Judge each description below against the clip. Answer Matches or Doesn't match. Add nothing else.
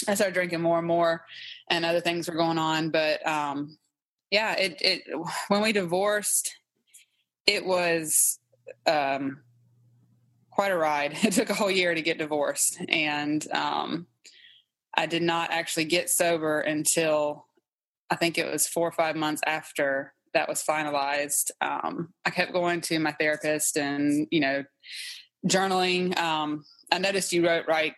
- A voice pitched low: Doesn't match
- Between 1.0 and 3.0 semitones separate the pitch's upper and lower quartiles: Matches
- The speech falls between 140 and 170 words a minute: Matches